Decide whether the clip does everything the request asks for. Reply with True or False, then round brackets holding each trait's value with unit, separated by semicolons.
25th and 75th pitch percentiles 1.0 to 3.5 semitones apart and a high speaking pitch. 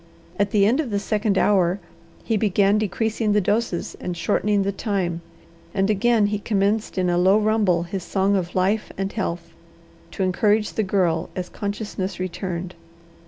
True (2.4 semitones; 200 Hz)